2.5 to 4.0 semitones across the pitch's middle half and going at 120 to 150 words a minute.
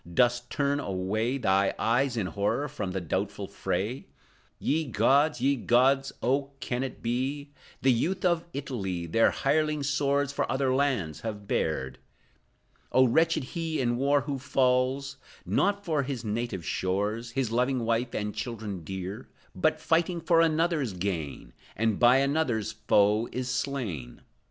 No: average, 4.9 semitones; average, 145 wpm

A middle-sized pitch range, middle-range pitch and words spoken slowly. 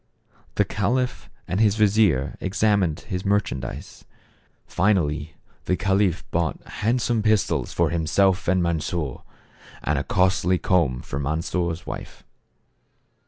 No: average, 4.3 semitones; very low, 90 Hz; slow, 125 wpm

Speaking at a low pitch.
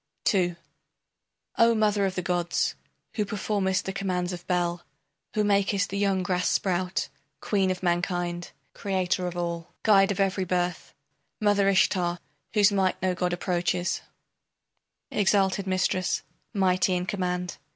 No: medium, 185 Hz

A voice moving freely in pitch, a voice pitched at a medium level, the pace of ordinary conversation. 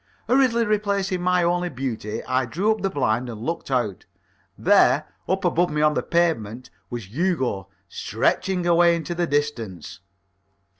Yes: wide, 6.8 semitones; medium, 165 Hz; average, 150 wpm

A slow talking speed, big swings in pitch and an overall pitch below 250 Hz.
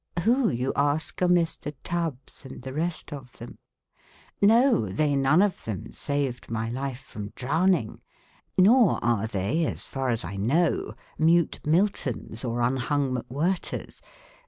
No: average, 145 wpm; wide, 5.9 semitones; medium, 140 Hz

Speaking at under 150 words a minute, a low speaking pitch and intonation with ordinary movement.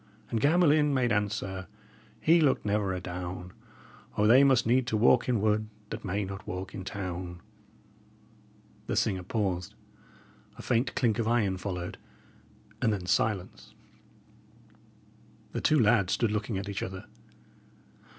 Yes: average, 140 wpm; low, 105 Hz; average, 4.1 semitones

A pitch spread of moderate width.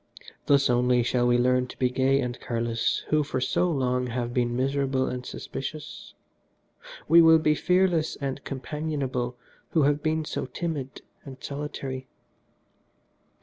Yes: average, 3.2 semitones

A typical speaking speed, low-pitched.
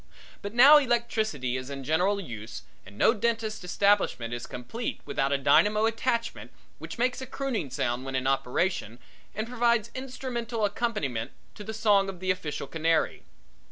No: average, 160 wpm; high, 200 Hz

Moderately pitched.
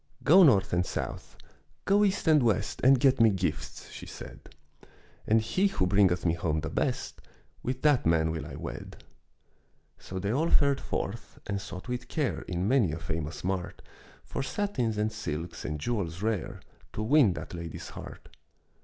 No: low, 105 Hz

